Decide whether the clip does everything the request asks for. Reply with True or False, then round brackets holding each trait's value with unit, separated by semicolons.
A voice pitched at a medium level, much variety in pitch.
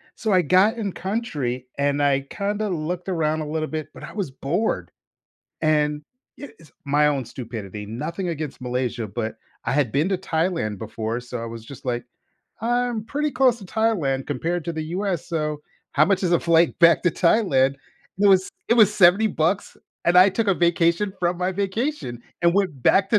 True (170 Hz; 6.0 semitones)